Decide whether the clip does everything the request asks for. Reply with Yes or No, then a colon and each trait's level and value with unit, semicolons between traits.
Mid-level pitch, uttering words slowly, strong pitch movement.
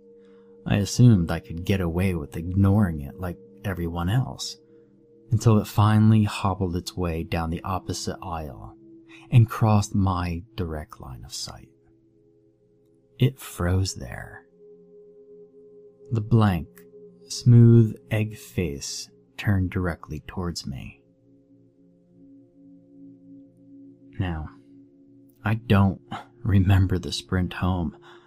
No: low, 105 Hz; slow, 100 wpm; wide, 7.1 semitones